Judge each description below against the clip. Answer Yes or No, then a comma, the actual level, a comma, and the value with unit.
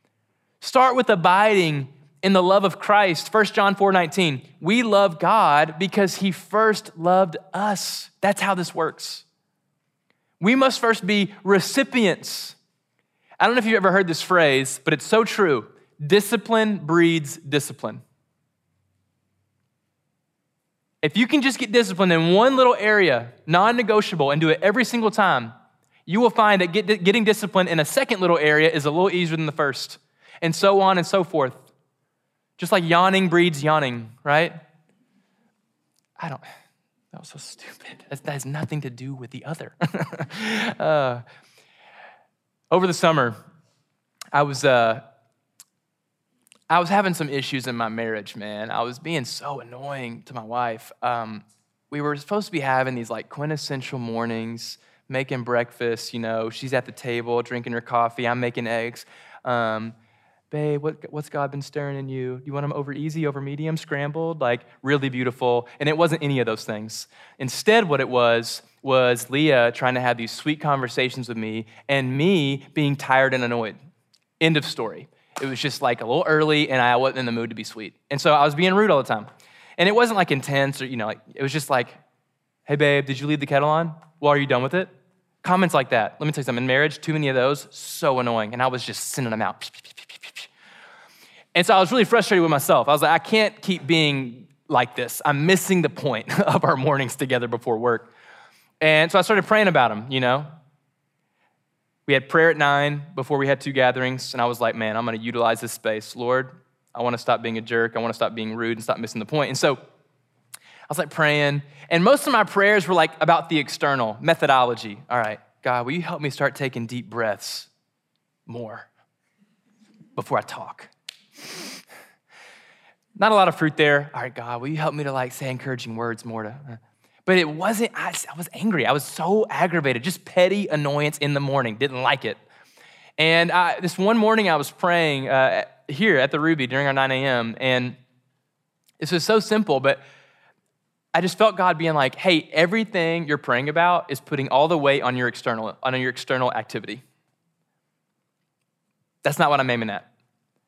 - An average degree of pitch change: No, wide, 5.9 semitones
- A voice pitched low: No, medium, 145 Hz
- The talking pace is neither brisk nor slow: Yes, average, 190 wpm